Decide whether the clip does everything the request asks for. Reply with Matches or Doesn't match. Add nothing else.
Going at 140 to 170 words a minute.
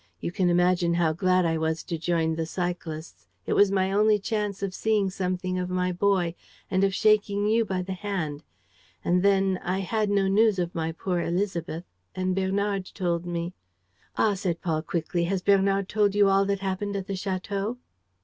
Doesn't match